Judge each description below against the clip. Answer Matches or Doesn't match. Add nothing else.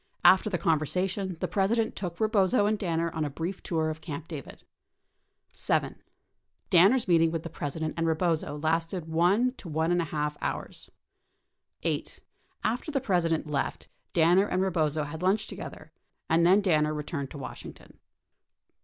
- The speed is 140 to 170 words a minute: Matches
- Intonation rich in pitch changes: Doesn't match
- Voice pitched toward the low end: Doesn't match